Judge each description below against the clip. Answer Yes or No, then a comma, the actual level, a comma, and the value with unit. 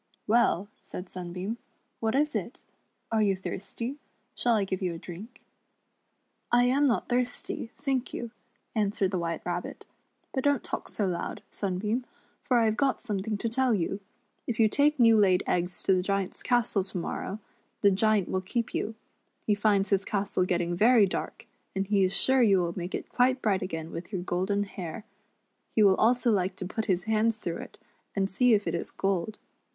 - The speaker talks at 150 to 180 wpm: No, average, 195 wpm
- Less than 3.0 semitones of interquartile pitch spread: No, average, 4.0 semitones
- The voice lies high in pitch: Yes, high, 205 Hz